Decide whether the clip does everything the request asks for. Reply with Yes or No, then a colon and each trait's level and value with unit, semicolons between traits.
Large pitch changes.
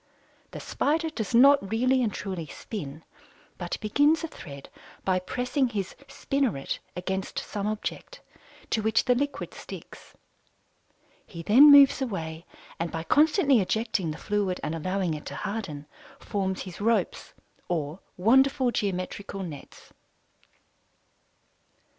Yes: wide, 6.3 semitones